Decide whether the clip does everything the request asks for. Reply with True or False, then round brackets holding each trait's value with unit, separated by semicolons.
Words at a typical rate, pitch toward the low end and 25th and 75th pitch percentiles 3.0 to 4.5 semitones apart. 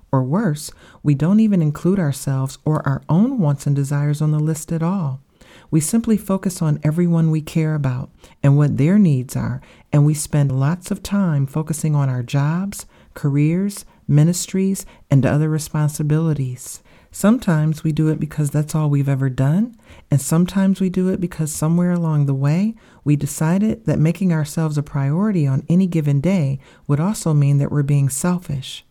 False (175 wpm; 155 Hz; 3.7 semitones)